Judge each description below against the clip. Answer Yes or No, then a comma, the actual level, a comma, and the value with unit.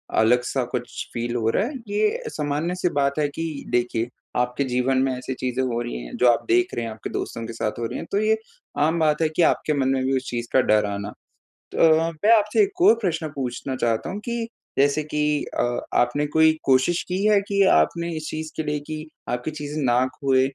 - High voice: No, medium, 140 Hz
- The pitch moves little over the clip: No, average, 4.8 semitones